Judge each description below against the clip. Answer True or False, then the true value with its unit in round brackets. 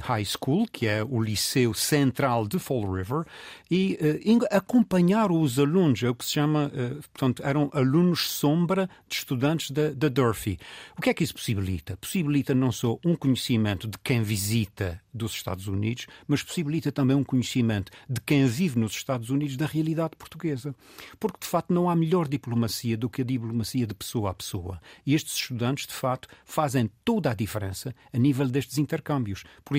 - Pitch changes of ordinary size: True (5.0 semitones)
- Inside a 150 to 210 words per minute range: True (180 wpm)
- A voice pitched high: False (135 Hz)